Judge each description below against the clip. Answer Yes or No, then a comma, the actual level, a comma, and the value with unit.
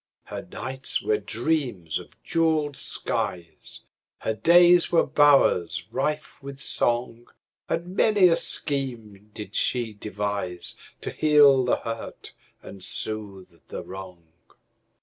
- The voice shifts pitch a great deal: Yes, wide, 6.7 semitones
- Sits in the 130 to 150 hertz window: No, low, 120 Hz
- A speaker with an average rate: No, slow, 105 wpm